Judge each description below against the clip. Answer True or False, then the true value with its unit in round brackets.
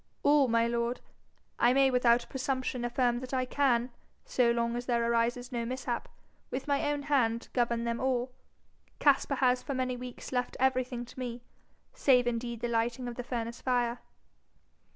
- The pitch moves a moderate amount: False (1.6 semitones)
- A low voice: False (245 Hz)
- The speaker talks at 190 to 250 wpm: False (170 wpm)